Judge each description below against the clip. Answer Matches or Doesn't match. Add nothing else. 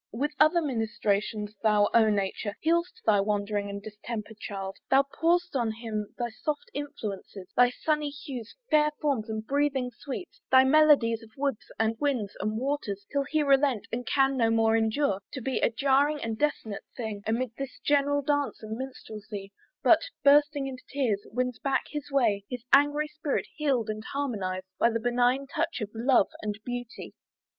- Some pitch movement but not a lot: Matches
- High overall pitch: Matches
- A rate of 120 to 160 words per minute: Doesn't match